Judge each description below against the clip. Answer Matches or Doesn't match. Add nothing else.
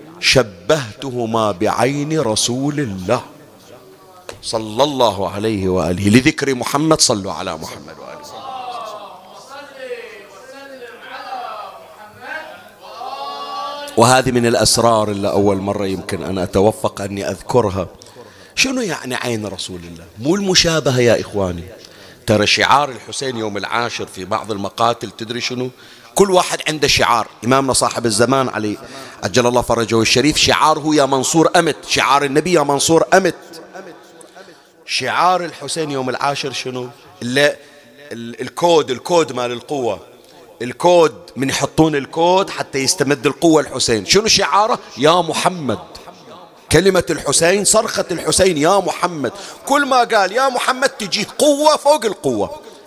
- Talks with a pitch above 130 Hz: Matches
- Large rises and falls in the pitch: Matches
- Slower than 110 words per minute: Doesn't match